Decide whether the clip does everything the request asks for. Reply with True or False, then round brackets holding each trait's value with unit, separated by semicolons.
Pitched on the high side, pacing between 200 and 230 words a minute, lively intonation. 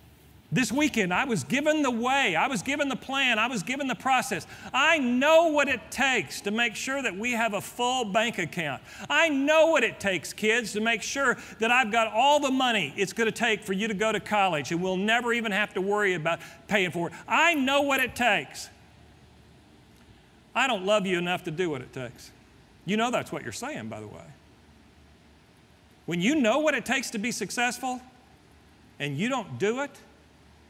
True (220 Hz; 205 wpm; 6.3 semitones)